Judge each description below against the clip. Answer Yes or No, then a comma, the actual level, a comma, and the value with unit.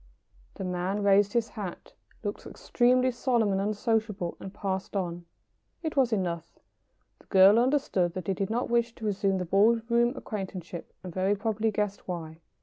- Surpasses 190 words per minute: No, average, 165 wpm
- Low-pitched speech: No, high, 200 Hz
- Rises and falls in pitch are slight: No, average, 3.6 semitones